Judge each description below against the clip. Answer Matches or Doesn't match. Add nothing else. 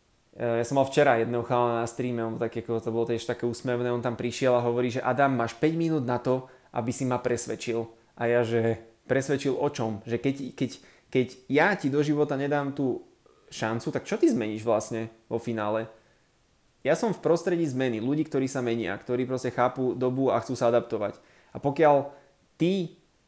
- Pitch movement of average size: Matches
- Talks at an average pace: Doesn't match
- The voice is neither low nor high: Doesn't match